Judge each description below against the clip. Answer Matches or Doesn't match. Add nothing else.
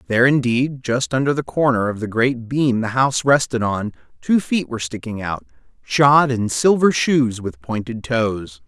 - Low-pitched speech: Matches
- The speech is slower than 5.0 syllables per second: Matches